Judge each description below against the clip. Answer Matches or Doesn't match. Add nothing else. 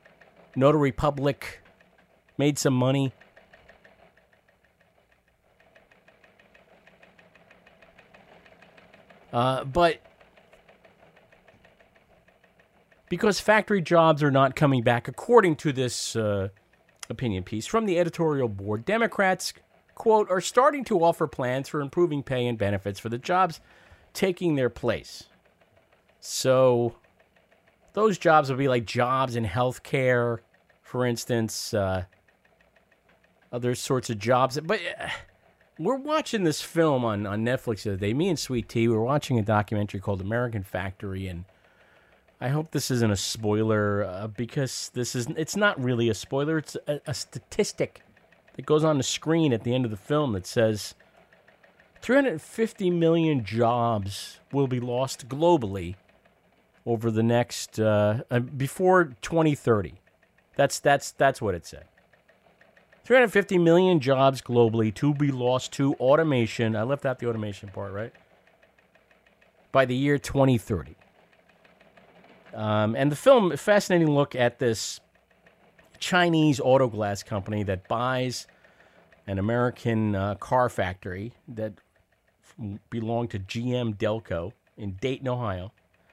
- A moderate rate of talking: Doesn't match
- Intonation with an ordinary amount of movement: Doesn't match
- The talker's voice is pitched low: Matches